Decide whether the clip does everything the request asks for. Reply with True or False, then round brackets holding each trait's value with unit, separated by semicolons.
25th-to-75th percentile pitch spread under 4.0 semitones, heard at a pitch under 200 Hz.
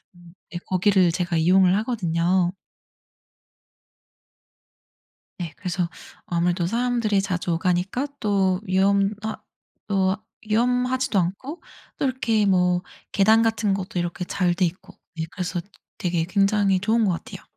True (3.2 semitones; 190 Hz)